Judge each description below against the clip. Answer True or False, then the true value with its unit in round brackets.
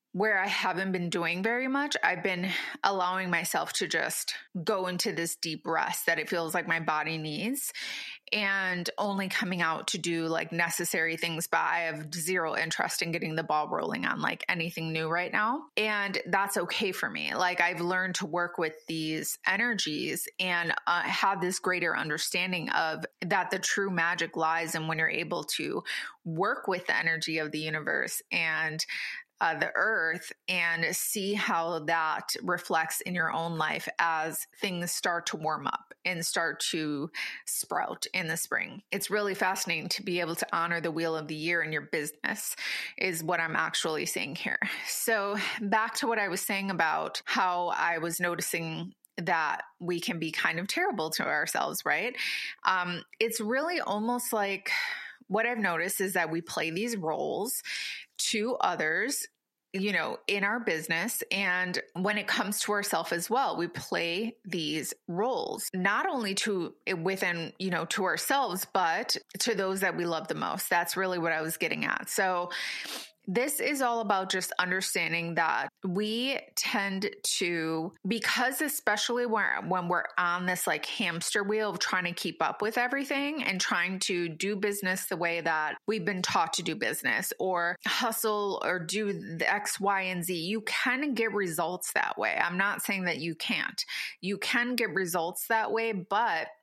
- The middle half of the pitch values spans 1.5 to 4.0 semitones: True (3.7 semitones)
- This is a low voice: False (185 Hz)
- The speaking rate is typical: True (175 wpm)